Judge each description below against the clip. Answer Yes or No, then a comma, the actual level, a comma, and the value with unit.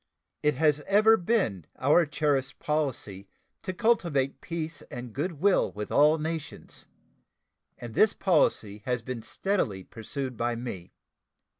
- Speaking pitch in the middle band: Yes, medium, 145 Hz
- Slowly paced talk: Yes, slow, 130 wpm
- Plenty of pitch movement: Yes, wide, 6.0 semitones